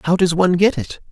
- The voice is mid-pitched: Yes, medium, 175 Hz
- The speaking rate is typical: No, fast, 270 wpm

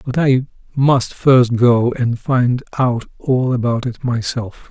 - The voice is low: Yes, low, 125 Hz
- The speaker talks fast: No, average, 155 wpm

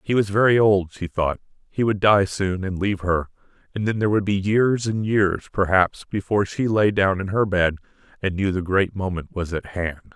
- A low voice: Yes, very low, 95 Hz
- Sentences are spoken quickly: Yes, fast, 220 wpm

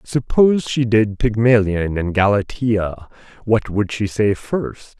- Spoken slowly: Yes, slow, 130 wpm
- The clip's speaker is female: No, male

